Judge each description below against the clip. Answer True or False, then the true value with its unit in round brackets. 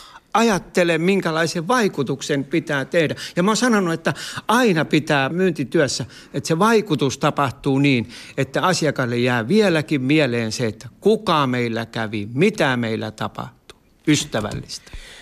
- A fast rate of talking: False (125 wpm)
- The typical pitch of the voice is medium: True (150 Hz)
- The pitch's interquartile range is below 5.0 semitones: False (5.5 semitones)